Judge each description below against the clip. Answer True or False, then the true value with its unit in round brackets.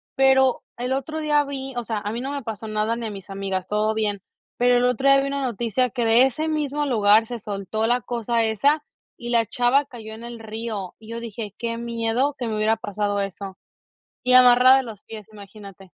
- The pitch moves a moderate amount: True (3.2 semitones)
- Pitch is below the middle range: False (230 Hz)